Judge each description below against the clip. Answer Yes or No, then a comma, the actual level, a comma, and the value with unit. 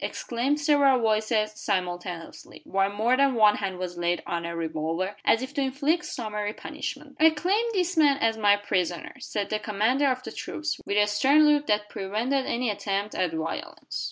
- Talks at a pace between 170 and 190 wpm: Yes, average, 185 wpm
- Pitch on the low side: No, high, 215 Hz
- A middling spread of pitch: No, wide, 6.1 semitones